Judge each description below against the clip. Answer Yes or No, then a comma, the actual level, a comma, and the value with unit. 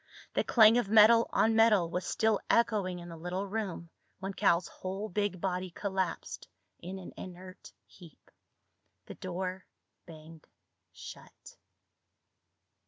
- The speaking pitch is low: No, high, 190 Hz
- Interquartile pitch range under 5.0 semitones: Yes, average, 2.9 semitones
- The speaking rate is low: Yes, slow, 125 wpm